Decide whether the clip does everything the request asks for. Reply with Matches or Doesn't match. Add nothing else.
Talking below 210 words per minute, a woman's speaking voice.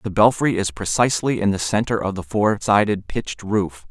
Doesn't match